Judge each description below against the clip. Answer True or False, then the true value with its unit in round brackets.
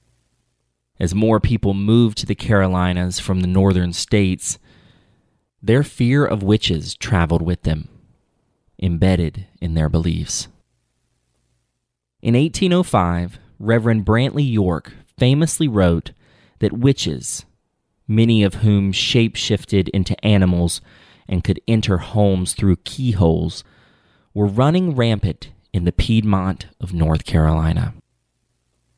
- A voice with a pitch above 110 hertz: False (100 Hz)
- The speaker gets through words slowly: True (110 wpm)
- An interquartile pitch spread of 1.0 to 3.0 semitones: False (4.5 semitones)